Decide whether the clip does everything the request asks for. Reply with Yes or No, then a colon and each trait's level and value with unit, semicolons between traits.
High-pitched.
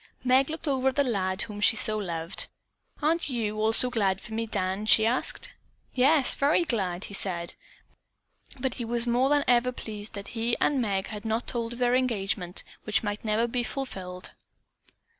Yes: high, 225 Hz